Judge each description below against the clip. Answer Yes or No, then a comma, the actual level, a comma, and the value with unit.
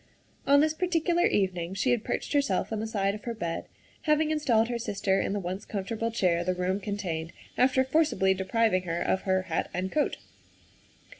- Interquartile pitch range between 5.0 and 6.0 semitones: Yes, wide, 5.6 semitones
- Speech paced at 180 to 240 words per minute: Yes, average, 190 wpm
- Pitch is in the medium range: No, high, 205 Hz